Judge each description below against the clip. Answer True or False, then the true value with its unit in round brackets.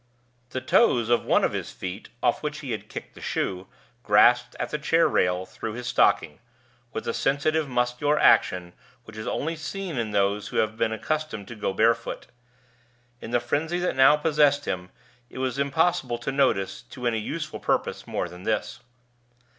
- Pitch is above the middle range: False (120 Hz)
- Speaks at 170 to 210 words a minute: True (180 wpm)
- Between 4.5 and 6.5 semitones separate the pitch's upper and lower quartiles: True (5.6 semitones)